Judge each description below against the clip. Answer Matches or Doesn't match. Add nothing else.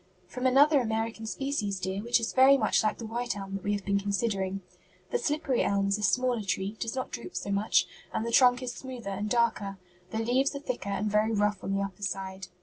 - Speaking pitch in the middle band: Doesn't match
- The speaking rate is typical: Doesn't match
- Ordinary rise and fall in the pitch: Matches